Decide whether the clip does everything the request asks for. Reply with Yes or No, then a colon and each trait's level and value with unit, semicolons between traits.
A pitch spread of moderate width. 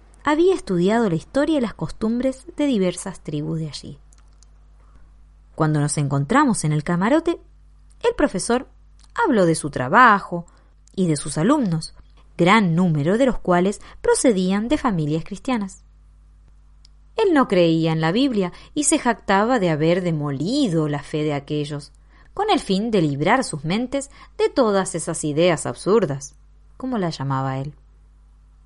No: wide, 8.9 semitones